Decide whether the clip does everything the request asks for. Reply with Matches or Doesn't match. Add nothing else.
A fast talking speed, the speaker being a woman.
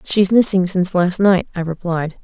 Doesn't match